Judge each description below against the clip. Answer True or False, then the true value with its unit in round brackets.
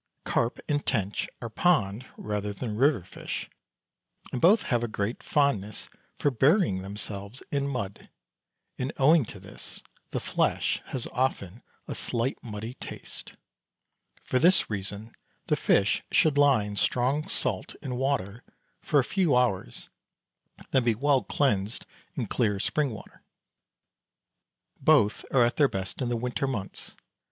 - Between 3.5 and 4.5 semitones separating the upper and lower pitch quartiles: False (5.1 semitones)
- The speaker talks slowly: False (145 wpm)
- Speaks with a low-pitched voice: True (120 Hz)